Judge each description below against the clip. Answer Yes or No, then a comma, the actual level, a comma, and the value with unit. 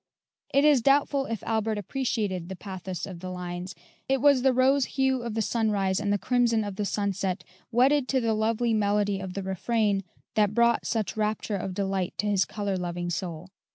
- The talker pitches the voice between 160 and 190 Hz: No, high, 210 Hz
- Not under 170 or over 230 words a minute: Yes, average, 190 wpm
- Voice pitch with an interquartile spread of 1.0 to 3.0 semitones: No, average, 3.7 semitones